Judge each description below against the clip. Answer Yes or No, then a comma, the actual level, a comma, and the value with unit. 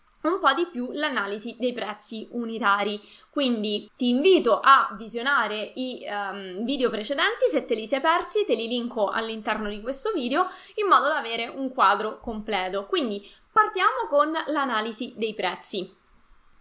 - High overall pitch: Yes, high, 245 Hz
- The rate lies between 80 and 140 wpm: No, average, 150 wpm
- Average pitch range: No, wide, 6.0 semitones